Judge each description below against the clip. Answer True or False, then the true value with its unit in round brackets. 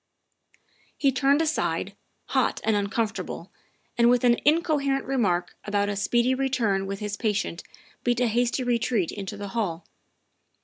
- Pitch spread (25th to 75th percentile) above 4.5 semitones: False (4.2 semitones)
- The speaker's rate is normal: True (160 wpm)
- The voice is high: True (235 Hz)